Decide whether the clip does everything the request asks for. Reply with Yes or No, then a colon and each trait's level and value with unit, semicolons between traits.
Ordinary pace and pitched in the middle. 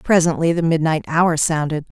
Yes: average, 150 wpm; medium, 160 Hz